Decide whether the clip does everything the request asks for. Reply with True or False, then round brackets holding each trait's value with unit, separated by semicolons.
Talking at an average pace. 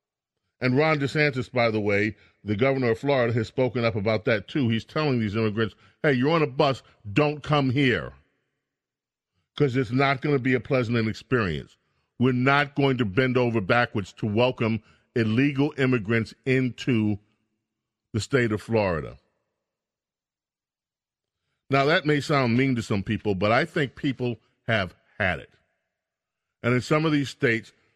True (160 wpm)